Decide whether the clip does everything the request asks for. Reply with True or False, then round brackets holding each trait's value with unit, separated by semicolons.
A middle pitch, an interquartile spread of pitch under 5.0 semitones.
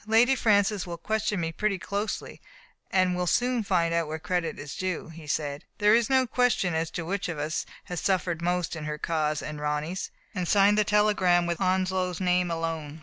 True (180 Hz; 3.8 semitones)